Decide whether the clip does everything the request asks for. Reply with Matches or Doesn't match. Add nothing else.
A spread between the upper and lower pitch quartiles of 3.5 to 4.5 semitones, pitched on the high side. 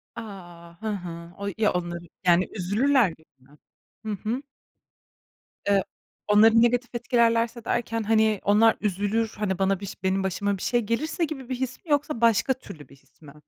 Matches